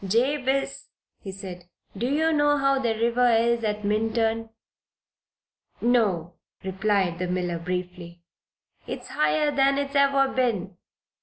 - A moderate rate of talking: No, slow, 125 wpm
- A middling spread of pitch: No, wide, 6.7 semitones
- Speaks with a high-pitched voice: Yes, high, 225 Hz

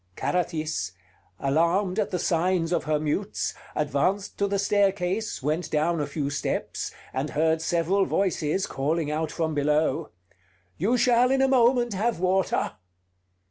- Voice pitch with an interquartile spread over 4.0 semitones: Yes, average, 4.5 semitones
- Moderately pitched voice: Yes, medium, 170 Hz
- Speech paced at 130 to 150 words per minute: Yes, average, 140 wpm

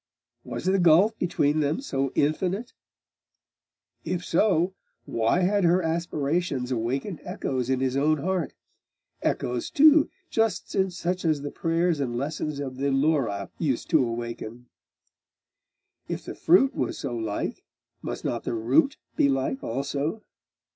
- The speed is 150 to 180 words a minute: No, slow, 135 wpm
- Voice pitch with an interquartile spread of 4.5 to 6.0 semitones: Yes, wide, 5.4 semitones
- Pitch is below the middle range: No, medium, 150 Hz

